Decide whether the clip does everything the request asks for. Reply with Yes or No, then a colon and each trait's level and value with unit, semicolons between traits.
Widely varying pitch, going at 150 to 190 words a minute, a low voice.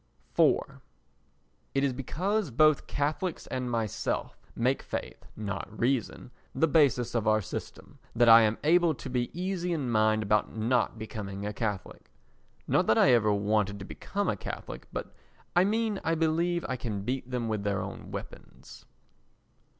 Yes: wide, 6.4 semitones; average, 160 wpm; low, 125 Hz